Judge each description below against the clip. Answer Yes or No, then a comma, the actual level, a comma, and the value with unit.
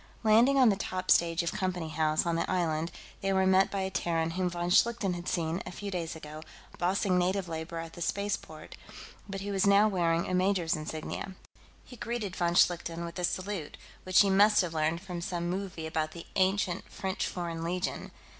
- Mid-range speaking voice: Yes, medium, 180 Hz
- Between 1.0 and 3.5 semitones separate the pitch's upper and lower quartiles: Yes, narrow, 2.6 semitones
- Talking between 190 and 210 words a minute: Yes, average, 200 wpm